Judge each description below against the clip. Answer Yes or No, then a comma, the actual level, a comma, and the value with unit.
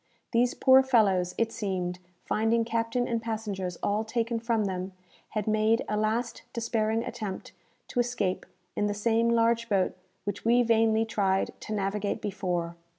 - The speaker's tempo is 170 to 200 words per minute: No, average, 150 wpm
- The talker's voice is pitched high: Yes, high, 220 Hz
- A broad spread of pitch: No, narrow, 2.5 semitones